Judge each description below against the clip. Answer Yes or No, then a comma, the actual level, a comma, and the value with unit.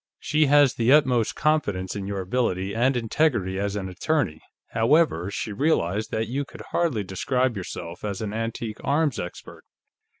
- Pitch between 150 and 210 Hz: No, low, 115 Hz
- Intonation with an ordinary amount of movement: No, wide, 6.1 semitones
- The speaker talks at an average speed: Yes, average, 160 wpm